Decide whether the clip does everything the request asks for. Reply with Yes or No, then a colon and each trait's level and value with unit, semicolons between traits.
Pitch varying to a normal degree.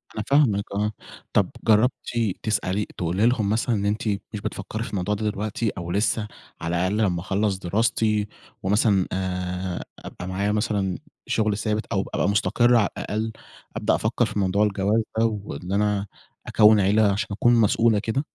No: narrow, 2.2 semitones